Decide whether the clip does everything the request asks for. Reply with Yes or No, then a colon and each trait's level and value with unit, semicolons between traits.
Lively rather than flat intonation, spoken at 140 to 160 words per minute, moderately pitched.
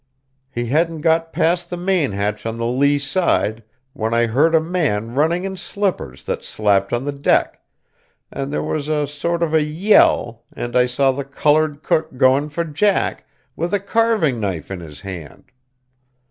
No: wide, 5.9 semitones; average, 175 wpm; medium, 145 Hz